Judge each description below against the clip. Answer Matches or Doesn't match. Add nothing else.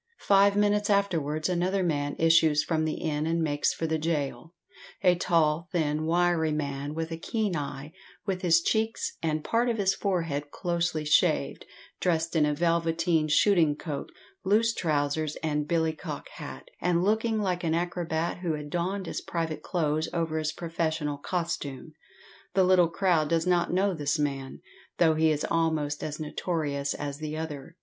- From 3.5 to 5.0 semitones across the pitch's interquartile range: Doesn't match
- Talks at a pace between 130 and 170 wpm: Matches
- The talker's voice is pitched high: Doesn't match